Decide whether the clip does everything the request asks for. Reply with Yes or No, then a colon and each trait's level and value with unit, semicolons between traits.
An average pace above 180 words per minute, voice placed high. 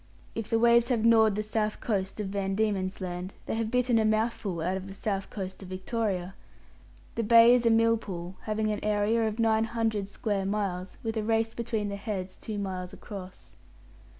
Yes: average, 195 wpm; high, 215 Hz